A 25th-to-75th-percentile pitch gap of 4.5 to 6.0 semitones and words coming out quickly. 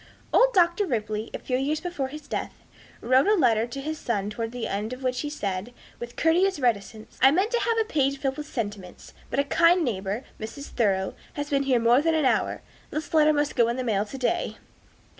Yes: average, 5.2 semitones; fast, 220 wpm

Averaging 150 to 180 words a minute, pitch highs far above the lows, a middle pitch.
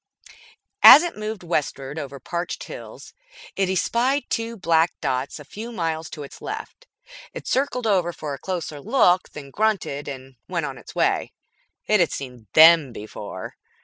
Yes: average, 160 wpm; wide, 7.2 semitones; medium, 170 Hz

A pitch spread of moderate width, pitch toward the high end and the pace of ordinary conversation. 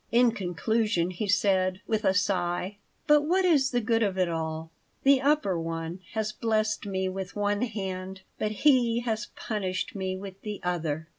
Yes: average, 3.6 semitones; high, 200 Hz; average, 170 wpm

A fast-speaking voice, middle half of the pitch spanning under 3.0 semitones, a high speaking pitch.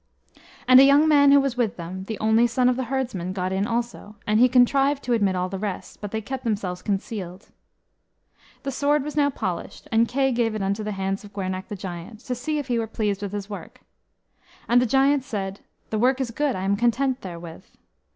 No: fast, 220 wpm; average, 4.9 semitones; high, 225 Hz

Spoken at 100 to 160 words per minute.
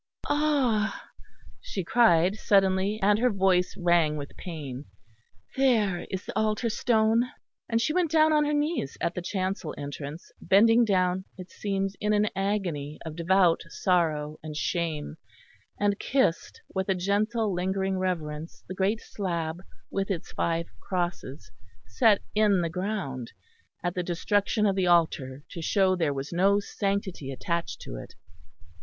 Yes: average, 150 wpm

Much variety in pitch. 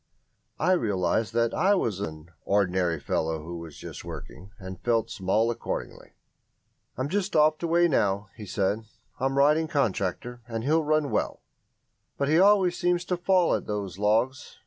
Yes: wide, 8.4 semitones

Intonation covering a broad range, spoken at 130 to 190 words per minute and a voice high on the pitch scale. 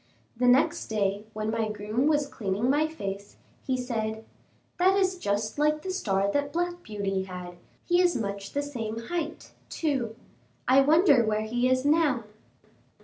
Yes: wide, 6.0 semitones; average, 160 wpm; high, 245 Hz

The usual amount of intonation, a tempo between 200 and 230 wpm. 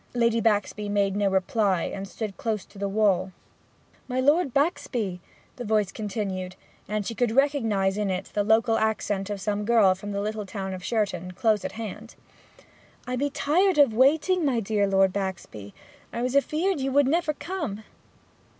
No: average, 4.3 semitones; average, 175 wpm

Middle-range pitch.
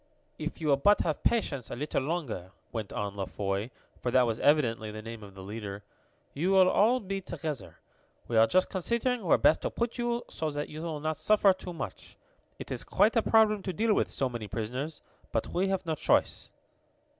Yes: medium, 155 Hz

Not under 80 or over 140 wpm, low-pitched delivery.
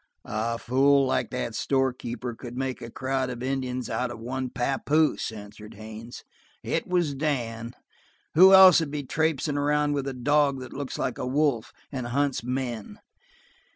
No: average, 165 wpm; low, 130 Hz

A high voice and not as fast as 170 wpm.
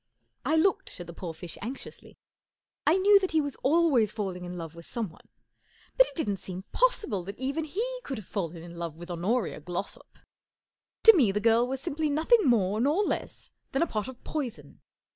No: high, 235 Hz; average, 195 wpm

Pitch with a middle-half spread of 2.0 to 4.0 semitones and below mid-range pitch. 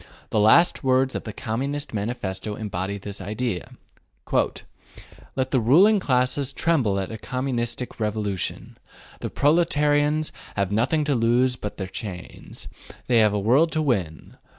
No: average, 5.1 semitones; low, 120 Hz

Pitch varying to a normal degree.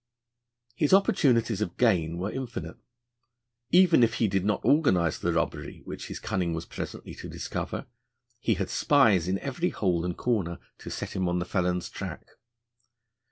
No: wide, 5.9 semitones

